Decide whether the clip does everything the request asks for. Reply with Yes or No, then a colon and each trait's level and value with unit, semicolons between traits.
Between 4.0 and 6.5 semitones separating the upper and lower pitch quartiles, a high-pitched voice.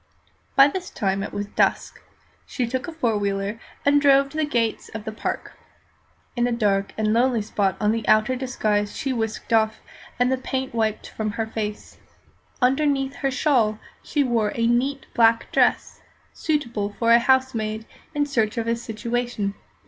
No: average, 3.4 semitones; high, 230 Hz